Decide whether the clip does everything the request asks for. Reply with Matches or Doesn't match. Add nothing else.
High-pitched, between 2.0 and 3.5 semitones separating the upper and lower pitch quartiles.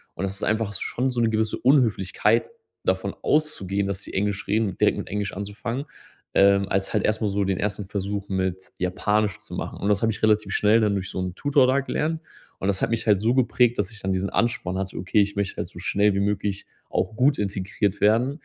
Doesn't match